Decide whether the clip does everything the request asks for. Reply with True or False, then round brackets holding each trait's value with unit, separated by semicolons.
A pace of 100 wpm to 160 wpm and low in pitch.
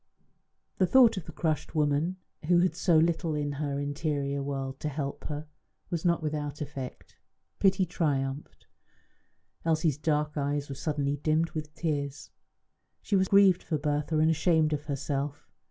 False (155 wpm; 150 Hz)